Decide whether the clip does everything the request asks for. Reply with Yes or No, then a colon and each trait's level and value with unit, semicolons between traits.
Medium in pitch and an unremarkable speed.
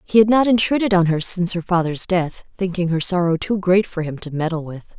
No: medium, 180 Hz; fast, 240 wpm